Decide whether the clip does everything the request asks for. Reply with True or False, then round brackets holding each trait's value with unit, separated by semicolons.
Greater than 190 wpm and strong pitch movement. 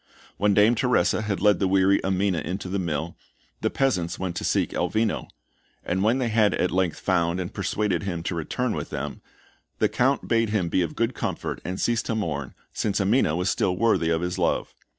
False (205 wpm; 3.8 semitones)